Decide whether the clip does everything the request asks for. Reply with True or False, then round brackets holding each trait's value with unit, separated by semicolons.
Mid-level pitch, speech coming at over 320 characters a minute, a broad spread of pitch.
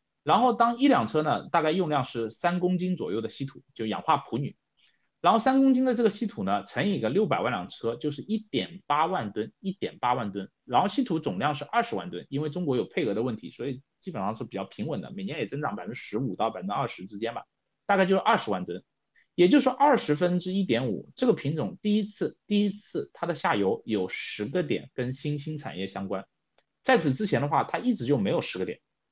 True (180 Hz; 340 characters per minute; 8.3 semitones)